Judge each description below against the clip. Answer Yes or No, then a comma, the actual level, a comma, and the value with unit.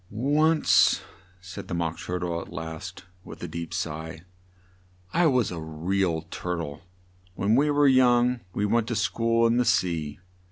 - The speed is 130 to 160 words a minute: No, average, 170 wpm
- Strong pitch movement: Yes, wide, 6.3 semitones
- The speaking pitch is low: Yes, very low, 95 Hz